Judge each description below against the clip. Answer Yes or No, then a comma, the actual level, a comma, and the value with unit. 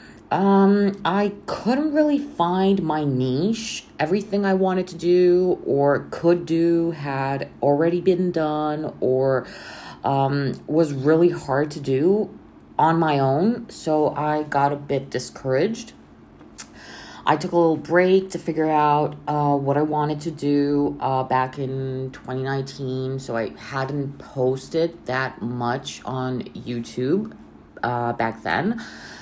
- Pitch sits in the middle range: Yes, medium, 150 Hz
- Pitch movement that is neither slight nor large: Yes, average, 4.8 semitones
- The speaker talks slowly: Yes, slow, 130 wpm